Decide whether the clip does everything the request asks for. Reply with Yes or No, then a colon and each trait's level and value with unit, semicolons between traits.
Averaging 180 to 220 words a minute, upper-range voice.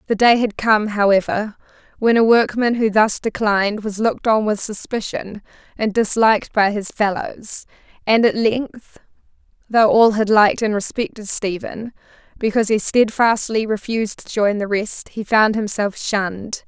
No: average, 150 wpm; high, 215 Hz